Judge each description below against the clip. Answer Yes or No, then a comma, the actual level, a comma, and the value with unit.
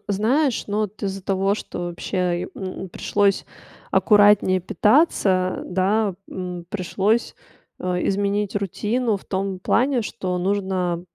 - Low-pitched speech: No, high, 195 Hz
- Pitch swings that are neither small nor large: No, narrow, 2.2 semitones